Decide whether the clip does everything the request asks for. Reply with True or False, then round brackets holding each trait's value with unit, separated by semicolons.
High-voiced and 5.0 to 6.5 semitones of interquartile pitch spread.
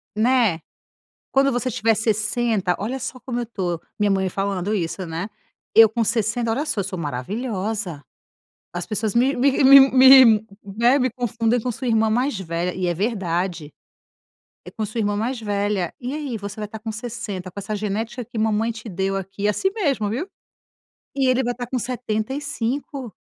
False (220 Hz; 3.7 semitones)